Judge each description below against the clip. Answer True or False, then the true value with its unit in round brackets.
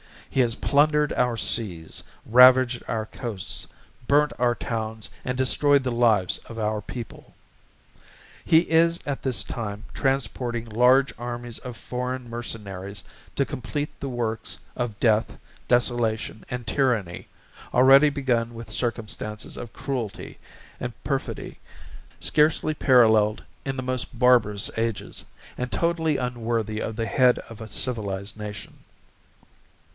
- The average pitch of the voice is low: True (120 Hz)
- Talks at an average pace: False (125 wpm)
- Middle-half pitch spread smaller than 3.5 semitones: True (2.9 semitones)